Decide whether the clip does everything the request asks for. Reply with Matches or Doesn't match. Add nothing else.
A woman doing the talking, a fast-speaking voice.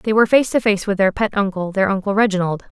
Matches